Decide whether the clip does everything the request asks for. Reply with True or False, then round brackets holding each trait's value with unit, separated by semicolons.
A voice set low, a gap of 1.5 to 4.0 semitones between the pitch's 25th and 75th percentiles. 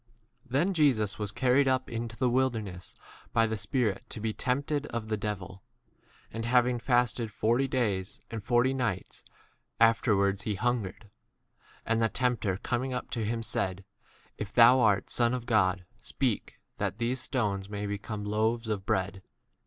True (115 Hz; 3.3 semitones)